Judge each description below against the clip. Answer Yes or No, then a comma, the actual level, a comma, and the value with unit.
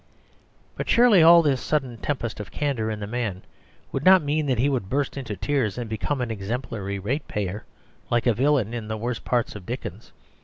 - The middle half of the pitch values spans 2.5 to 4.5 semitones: No, average, 5.0 semitones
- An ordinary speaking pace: Yes, average, 195 wpm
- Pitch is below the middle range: Yes, low, 120 Hz